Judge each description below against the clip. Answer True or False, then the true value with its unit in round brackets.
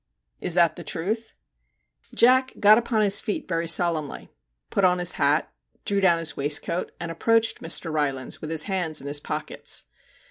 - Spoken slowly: False (175 wpm)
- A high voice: False (170 Hz)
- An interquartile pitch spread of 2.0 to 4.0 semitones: False (4.6 semitones)